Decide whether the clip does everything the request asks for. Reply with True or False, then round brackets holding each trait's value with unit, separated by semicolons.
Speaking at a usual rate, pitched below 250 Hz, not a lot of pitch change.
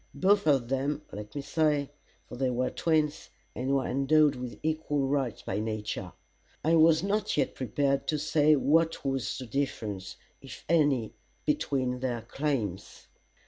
False (150 wpm; 140 Hz; 3.5 semitones)